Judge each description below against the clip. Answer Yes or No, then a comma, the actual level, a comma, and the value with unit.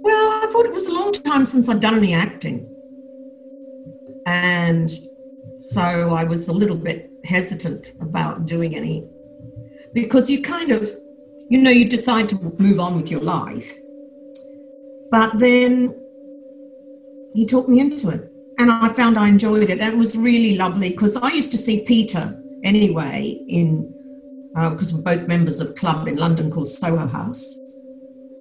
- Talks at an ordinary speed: Yes, average, 165 wpm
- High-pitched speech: Yes, high, 235 Hz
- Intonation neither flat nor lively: No, wide, 7.3 semitones